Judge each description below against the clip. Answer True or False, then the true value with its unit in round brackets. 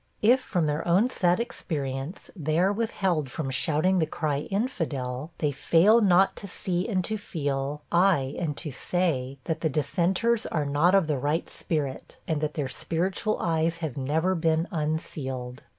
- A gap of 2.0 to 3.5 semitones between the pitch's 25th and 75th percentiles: False (4.2 semitones)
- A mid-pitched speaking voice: True (160 Hz)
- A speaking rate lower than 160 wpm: False (170 wpm)